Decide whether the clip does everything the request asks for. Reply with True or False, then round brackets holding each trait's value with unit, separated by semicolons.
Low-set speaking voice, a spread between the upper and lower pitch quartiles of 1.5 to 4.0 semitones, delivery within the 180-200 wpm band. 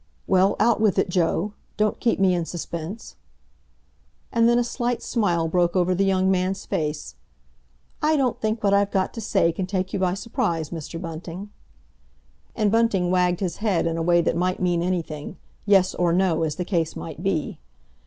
False (185 Hz; 3.1 semitones; 185 wpm)